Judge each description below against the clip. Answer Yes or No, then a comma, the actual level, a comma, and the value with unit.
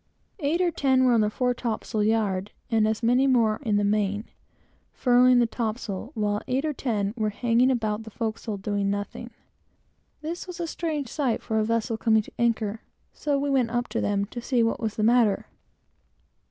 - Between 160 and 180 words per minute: No, average, 195 wpm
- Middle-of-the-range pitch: No, high, 230 Hz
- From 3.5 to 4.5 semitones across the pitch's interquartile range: No, average, 3.0 semitones